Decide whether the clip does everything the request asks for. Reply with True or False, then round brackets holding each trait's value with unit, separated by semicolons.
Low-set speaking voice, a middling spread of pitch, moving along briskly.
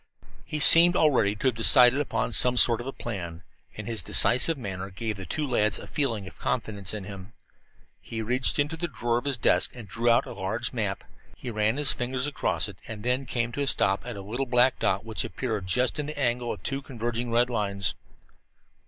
True (120 Hz; 3.7 semitones; 215 wpm)